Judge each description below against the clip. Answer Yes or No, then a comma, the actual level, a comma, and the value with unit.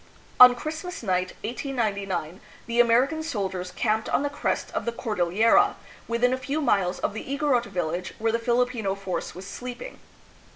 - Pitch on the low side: No, high, 230 Hz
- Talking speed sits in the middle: Yes, average, 170 wpm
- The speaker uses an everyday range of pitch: Yes, average, 4.8 semitones